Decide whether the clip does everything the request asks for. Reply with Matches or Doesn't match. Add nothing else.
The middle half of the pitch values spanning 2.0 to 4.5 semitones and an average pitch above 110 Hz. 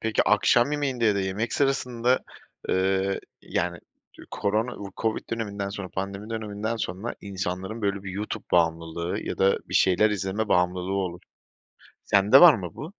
Doesn't match